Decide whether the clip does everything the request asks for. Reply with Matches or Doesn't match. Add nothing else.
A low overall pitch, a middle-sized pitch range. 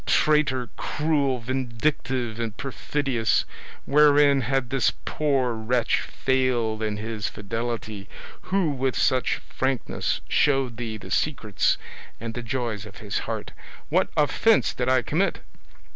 Matches